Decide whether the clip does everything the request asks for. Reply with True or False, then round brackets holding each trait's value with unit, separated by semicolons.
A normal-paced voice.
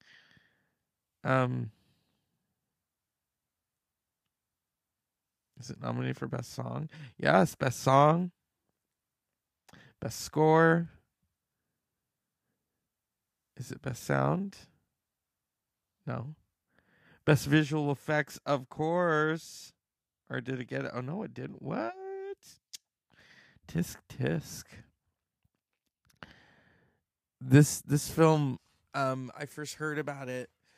False (85 wpm)